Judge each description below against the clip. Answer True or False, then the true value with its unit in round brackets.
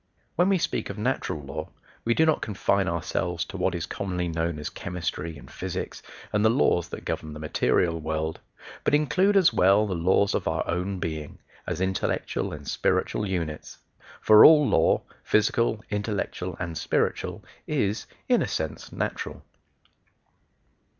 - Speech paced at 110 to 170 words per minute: True (155 wpm)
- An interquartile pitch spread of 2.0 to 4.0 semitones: False (4.5 semitones)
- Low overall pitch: True (95 Hz)